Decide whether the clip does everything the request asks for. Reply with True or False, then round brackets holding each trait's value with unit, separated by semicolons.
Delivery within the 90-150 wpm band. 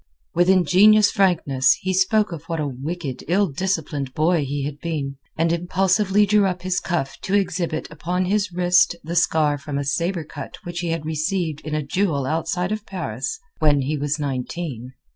False (180 wpm)